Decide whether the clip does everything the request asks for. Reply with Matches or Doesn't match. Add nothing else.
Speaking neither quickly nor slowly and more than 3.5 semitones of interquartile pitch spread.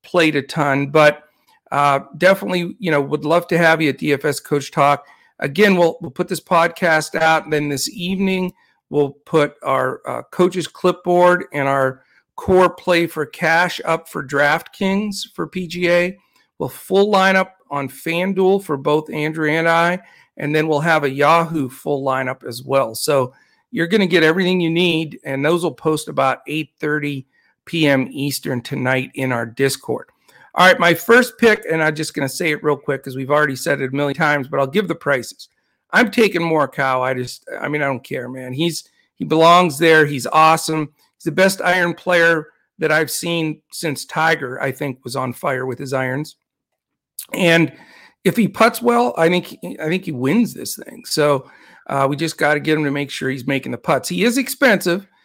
Matches